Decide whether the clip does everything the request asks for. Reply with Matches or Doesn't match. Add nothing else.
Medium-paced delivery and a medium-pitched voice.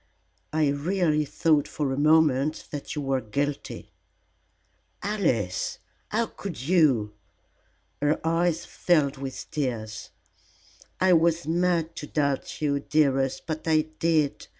Doesn't match